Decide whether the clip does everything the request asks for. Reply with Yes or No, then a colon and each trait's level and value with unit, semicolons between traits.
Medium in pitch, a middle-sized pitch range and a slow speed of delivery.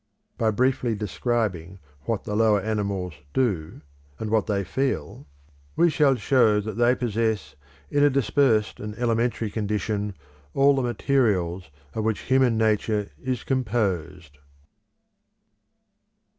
No: low, 110 Hz; average, 3.4 semitones; slow, 120 wpm